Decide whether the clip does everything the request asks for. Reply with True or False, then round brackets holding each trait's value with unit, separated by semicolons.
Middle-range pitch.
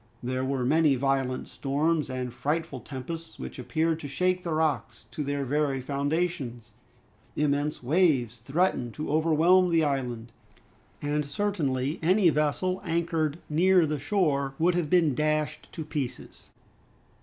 True (150 Hz)